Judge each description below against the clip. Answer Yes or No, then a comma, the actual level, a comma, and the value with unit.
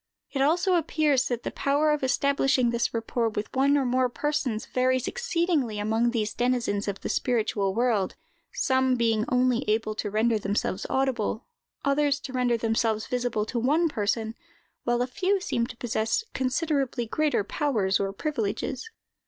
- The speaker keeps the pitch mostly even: No, average, 3.9 semitones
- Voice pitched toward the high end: Yes, high, 245 Hz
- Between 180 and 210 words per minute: No, average, 160 wpm